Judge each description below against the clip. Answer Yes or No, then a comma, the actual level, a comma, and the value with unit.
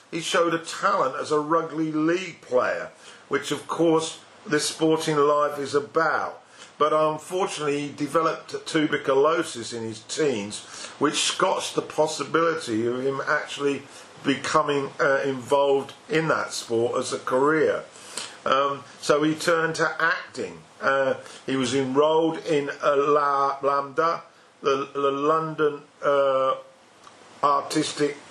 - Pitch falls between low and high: Yes, medium, 145 Hz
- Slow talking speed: Yes, slow, 130 wpm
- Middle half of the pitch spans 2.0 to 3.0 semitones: Yes, narrow, 2.5 semitones